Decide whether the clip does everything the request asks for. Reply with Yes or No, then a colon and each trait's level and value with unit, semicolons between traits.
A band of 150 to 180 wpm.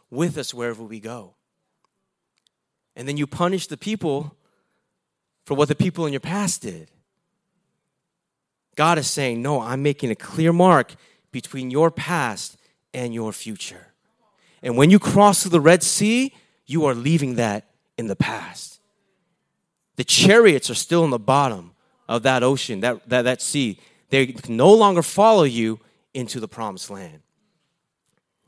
Yes: average, 155 wpm